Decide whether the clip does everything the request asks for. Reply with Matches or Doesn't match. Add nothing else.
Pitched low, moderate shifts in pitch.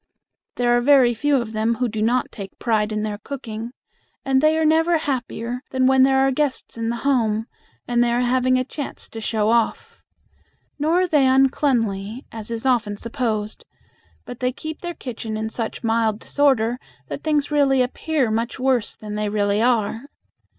Doesn't match